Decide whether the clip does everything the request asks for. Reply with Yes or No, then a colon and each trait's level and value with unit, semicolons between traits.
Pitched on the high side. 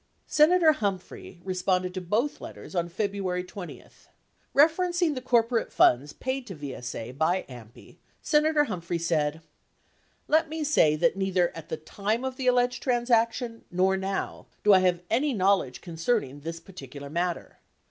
Yes: high, 195 Hz